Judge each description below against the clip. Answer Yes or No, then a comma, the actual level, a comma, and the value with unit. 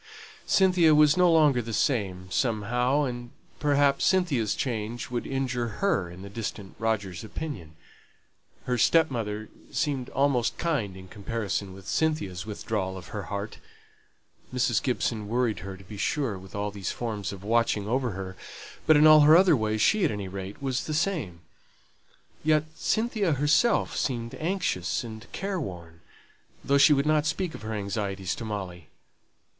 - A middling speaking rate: Yes, average, 160 wpm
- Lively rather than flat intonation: Yes, wide, 6.7 semitones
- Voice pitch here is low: Yes, low, 115 Hz